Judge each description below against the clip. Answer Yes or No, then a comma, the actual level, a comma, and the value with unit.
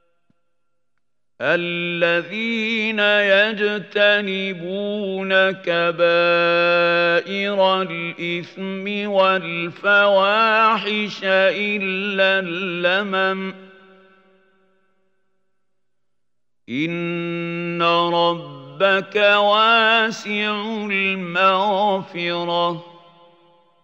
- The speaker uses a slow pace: Yes, slow, 30 wpm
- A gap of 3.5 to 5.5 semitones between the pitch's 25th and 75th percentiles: No, average, 2.8 semitones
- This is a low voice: No, high, 190 Hz